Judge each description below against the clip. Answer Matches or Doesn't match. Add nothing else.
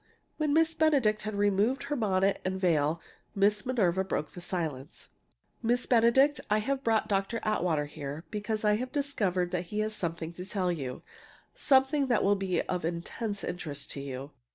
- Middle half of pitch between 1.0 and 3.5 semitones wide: Doesn't match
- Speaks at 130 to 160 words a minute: Doesn't match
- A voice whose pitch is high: Matches